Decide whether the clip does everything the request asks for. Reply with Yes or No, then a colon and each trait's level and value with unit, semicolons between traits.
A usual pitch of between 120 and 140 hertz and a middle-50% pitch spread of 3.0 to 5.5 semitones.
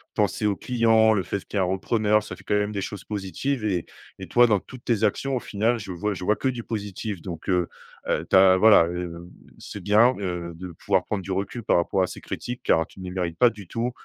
No: low, 100 Hz; average, 3.5 semitones